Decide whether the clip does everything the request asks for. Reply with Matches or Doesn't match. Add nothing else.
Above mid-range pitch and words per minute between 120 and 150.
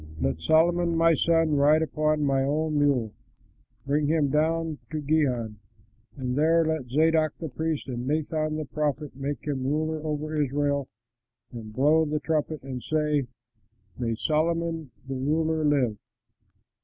Doesn't match